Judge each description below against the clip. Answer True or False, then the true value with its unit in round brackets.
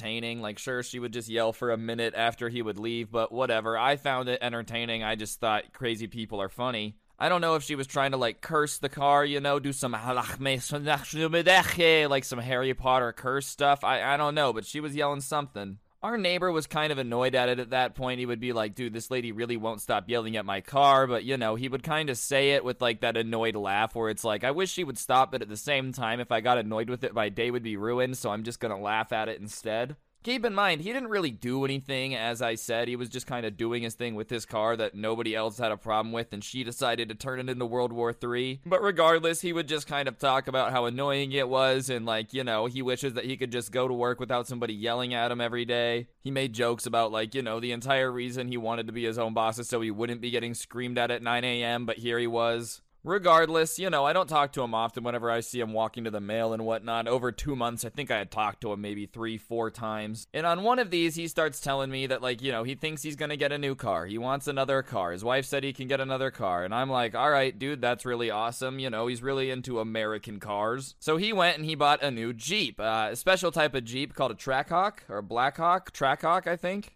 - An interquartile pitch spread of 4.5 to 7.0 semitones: False (3.2 semitones)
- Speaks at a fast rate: True (265 wpm)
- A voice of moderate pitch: False (125 Hz)